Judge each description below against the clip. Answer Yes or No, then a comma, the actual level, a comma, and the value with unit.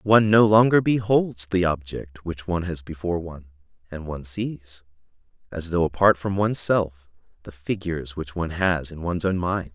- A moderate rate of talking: Yes, average, 180 wpm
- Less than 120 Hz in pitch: Yes, very low, 90 Hz